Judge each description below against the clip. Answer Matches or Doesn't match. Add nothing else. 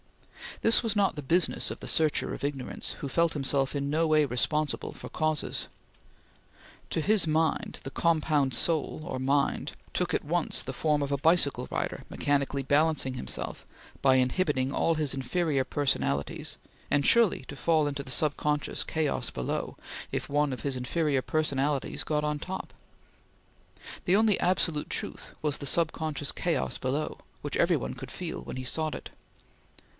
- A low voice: Doesn't match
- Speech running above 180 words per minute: Doesn't match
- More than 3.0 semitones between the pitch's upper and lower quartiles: Doesn't match